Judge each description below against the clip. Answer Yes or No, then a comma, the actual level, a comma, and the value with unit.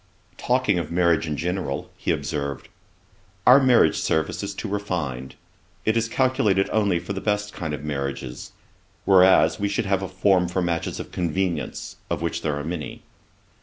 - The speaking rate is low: No, average, 165 wpm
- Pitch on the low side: Yes, very low, 90 Hz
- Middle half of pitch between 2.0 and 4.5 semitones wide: Yes, average, 4.2 semitones